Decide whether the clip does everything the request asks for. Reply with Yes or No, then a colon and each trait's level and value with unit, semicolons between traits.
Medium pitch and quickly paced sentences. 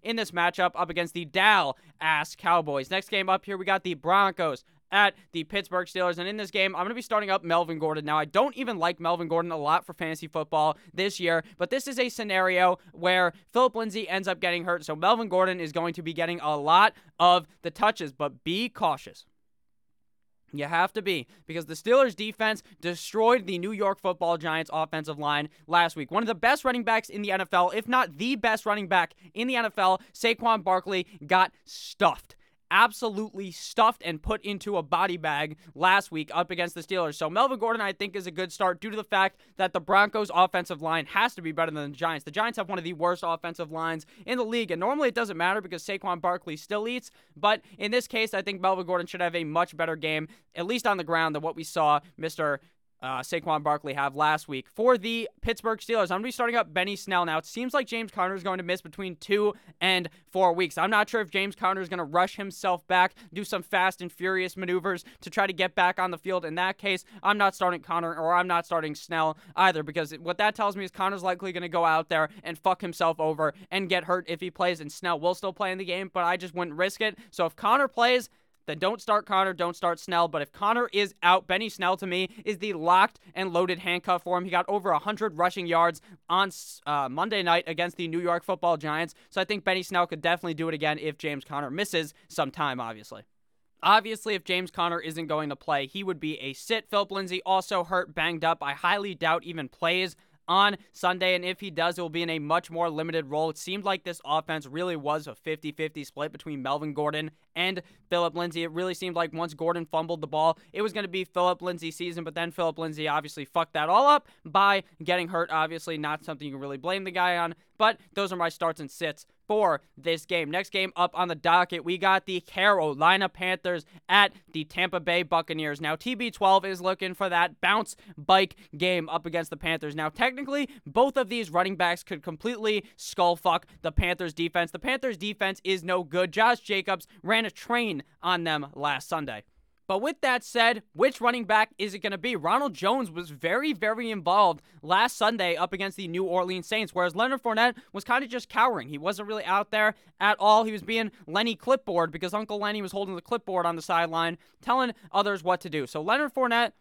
Yes: medium, 180 Hz; fast, 225 wpm